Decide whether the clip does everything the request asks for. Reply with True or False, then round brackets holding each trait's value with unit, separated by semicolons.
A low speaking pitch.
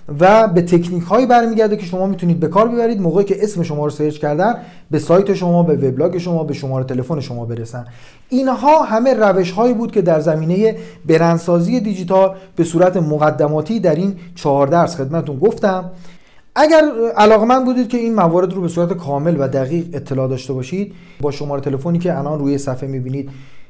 False (175 Hz)